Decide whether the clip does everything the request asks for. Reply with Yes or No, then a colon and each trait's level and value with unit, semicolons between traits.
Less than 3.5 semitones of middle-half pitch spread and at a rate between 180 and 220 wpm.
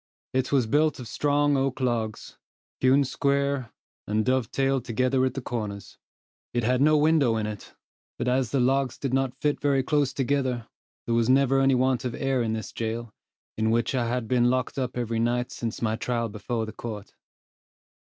Yes: average, 2.7 semitones; average, 185 wpm